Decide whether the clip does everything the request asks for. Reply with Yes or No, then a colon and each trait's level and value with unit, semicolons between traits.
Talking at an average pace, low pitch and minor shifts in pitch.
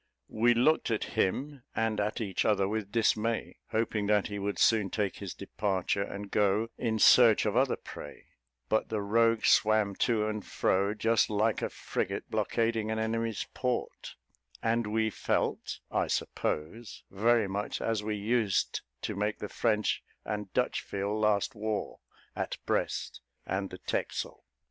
Yes: average, 155 wpm; low, 110 Hz; narrow, 1.9 semitones